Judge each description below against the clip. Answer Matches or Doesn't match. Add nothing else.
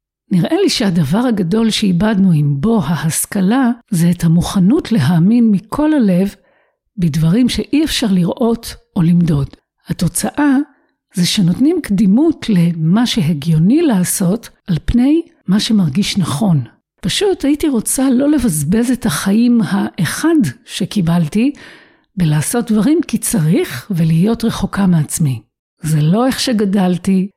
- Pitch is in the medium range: Doesn't match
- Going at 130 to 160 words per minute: Doesn't match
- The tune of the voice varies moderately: Doesn't match